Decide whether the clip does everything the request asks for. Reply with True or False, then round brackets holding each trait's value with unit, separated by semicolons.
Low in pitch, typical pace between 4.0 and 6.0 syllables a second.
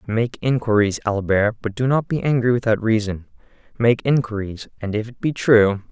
True (115 Hz; 5.0 syllables/s)